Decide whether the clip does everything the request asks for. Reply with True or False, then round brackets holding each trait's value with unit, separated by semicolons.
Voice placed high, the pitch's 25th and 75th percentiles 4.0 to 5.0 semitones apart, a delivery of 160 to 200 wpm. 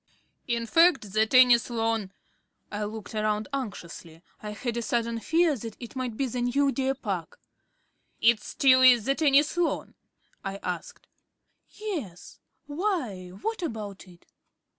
False (235 Hz; 4.6 semitones; 145 wpm)